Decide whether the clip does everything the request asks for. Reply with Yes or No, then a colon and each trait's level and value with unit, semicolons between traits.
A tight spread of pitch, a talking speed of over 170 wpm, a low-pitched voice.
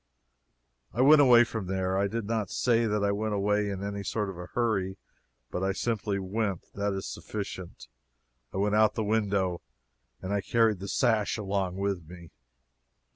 Yes: narrow, 2.3 semitones; average, 180 wpm; low, 100 Hz